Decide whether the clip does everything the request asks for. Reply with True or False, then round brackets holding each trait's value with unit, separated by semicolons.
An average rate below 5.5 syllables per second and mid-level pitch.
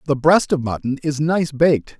True (5.1 syllables/s; 145 Hz)